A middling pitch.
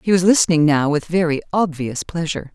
Yes: medium, 165 Hz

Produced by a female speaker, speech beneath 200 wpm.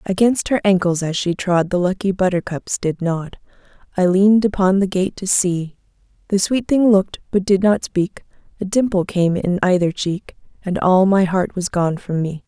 Yes: female; average, 190 wpm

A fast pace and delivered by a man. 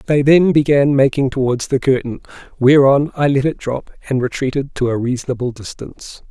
No: average, 170 wpm; male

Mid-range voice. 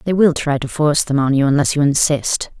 Yes: medium, 145 Hz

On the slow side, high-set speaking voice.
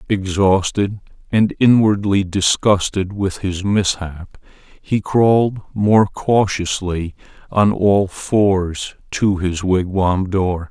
No: slow, 100 wpm; low, 100 Hz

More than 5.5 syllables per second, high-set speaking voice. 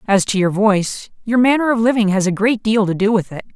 Yes: 6.0 syllables/s; high, 210 Hz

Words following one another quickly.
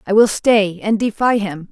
Yes: fast, 210 wpm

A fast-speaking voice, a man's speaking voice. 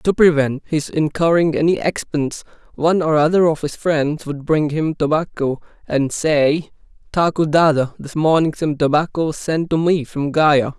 No: average, 165 wpm; male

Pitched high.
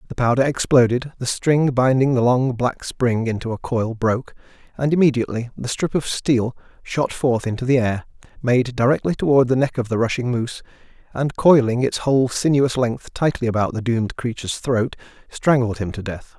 No: low, 125 Hz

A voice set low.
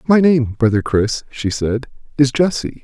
Yes: low, 130 Hz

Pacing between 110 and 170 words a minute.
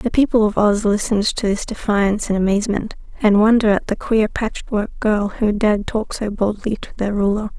No: average, 200 wpm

